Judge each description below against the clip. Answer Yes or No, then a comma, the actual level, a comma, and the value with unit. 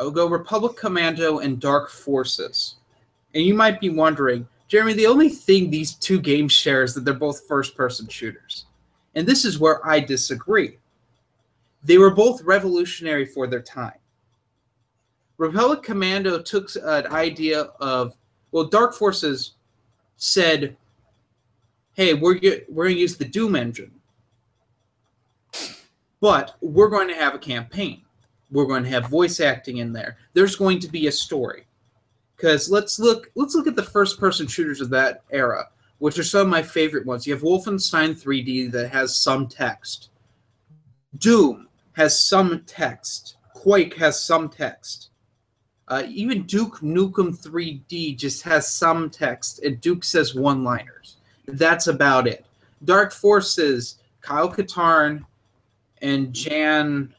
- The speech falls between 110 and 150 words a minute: Yes, average, 145 wpm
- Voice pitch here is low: No, medium, 145 Hz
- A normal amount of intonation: No, wide, 6.3 semitones